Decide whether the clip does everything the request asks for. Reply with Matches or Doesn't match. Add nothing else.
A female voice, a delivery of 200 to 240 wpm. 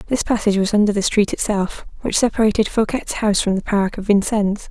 Matches